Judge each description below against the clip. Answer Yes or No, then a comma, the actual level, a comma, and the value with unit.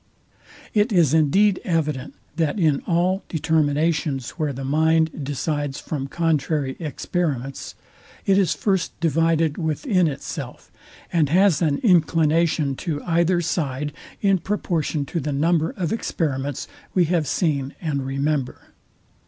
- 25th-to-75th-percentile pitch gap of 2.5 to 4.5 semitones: Yes, average, 3.0 semitones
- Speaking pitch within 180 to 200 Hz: No, medium, 160 Hz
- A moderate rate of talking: No, slow, 125 wpm